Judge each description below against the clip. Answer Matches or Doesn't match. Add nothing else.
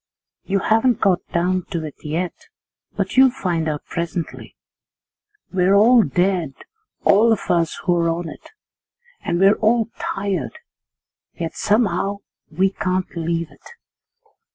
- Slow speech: Matches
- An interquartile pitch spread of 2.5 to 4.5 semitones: Matches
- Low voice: Doesn't match